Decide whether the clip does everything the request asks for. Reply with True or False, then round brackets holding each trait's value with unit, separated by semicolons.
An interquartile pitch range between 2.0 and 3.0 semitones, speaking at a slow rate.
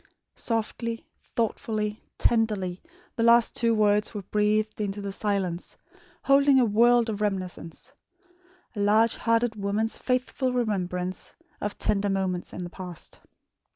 True (2.6 semitones; 125 wpm)